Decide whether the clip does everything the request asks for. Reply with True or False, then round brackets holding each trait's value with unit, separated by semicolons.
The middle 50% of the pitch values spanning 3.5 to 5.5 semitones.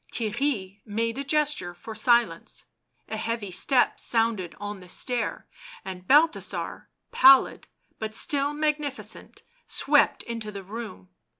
True (5.0 semitones)